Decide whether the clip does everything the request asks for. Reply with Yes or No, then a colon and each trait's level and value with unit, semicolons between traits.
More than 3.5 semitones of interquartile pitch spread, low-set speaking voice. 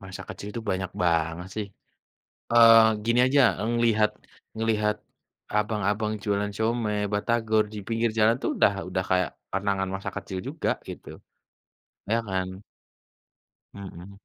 No: average, 2.8 semitones; low, 105 Hz